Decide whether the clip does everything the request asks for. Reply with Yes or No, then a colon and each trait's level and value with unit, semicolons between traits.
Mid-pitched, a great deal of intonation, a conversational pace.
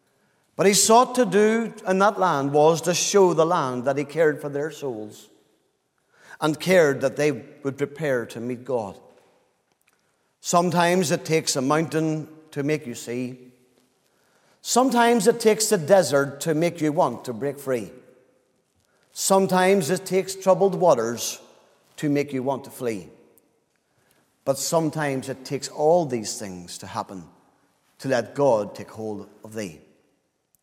Yes: medium, 150 Hz; wide, 6.3 semitones; average, 150 wpm